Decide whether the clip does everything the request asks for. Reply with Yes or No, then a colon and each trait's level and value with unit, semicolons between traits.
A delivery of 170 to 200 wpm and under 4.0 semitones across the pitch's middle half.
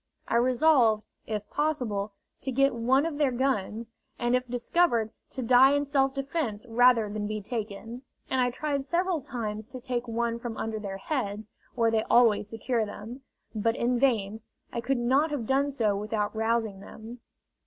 Yes: average, 175 wpm; average, 3.5 semitones